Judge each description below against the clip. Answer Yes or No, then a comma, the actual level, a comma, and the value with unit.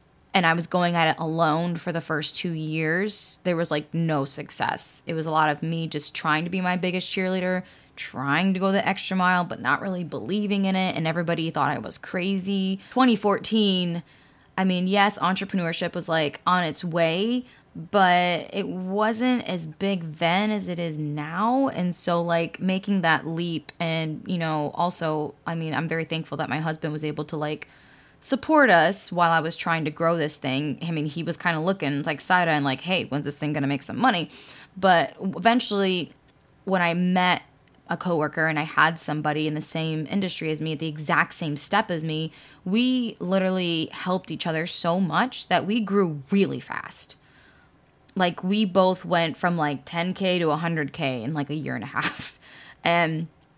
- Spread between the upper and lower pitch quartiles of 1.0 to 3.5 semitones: Yes, average, 3.2 semitones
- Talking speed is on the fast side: No, average, 195 wpm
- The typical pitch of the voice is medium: Yes, medium, 170 Hz